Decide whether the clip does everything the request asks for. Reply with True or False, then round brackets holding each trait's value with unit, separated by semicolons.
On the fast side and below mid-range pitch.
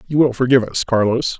True (215 wpm; 125 Hz)